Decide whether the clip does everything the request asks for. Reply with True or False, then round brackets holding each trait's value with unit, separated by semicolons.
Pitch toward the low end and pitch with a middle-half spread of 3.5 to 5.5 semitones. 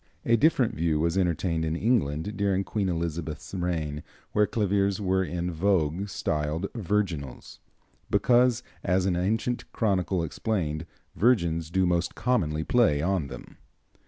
True (90 Hz; 4.0 semitones)